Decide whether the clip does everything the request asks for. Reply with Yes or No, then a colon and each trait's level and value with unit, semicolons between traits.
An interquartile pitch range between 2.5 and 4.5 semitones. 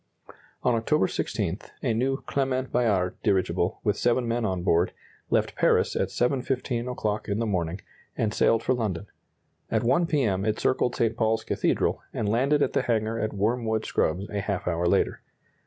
Yes: average, 3.6 semitones